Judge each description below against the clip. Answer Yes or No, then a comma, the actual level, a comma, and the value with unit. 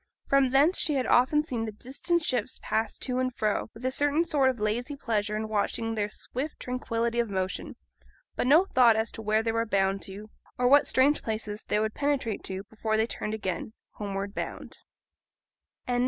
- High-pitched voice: Yes, high, 230 Hz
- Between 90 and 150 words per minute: No, average, 190 wpm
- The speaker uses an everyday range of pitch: Yes, average, 3.6 semitones